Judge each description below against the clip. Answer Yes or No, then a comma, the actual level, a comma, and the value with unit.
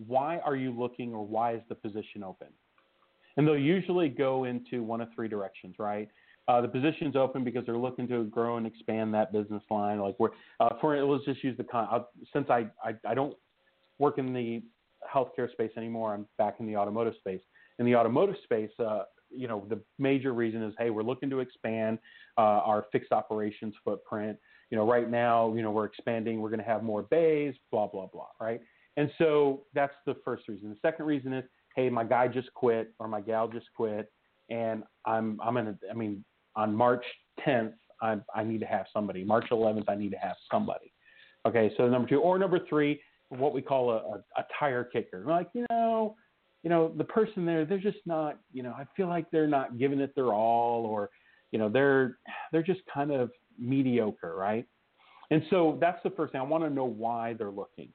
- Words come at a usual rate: No, fast, 210 wpm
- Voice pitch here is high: No, low, 120 Hz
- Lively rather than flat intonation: No, average, 4.3 semitones